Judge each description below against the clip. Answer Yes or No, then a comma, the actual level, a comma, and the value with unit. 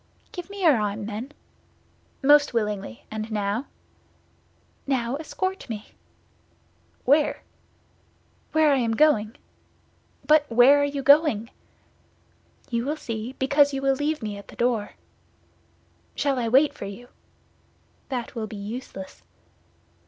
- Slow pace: Yes, slow, 125 wpm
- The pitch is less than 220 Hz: No, very high, 250 Hz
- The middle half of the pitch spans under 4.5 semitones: No, average, 4.9 semitones